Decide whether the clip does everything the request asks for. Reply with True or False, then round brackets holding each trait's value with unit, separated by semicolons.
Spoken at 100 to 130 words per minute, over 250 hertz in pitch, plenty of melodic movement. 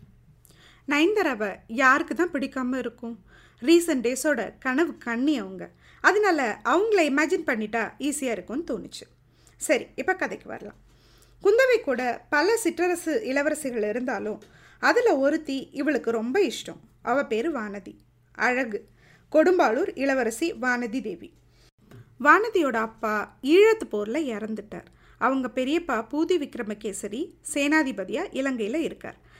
True (105 wpm; 270 Hz; 6.0 semitones)